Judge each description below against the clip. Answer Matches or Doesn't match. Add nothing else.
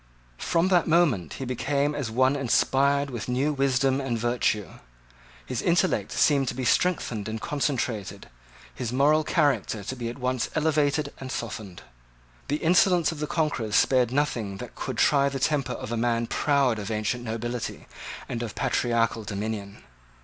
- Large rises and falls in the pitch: Doesn't match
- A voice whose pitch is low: Matches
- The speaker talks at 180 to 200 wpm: Doesn't match